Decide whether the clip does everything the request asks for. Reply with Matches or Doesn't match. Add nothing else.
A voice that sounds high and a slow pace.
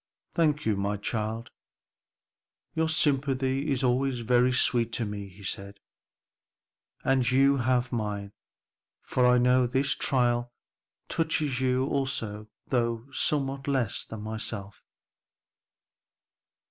Doesn't match